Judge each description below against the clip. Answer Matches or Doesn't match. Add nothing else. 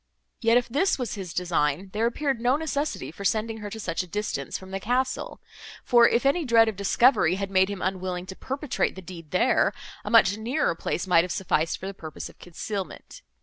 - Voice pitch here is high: Matches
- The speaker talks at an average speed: Doesn't match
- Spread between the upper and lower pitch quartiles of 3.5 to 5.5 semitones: Matches